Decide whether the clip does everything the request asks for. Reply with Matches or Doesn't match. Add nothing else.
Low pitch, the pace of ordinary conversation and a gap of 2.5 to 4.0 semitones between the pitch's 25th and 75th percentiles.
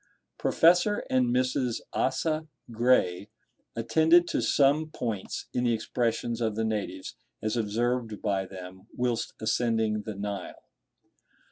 Doesn't match